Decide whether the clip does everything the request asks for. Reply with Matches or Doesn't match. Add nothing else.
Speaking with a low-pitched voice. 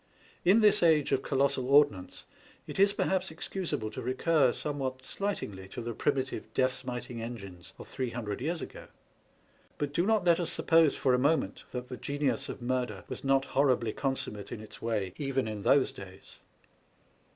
Matches